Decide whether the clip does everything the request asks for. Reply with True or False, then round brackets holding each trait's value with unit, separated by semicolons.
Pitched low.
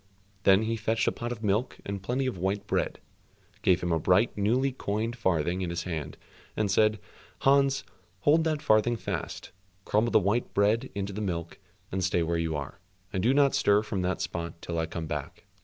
True (100 Hz)